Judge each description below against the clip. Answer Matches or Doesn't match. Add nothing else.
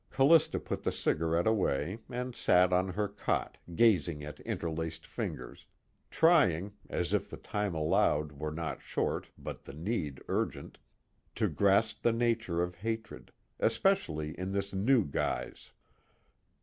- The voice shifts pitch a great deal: Matches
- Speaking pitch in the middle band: Doesn't match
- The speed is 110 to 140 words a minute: Matches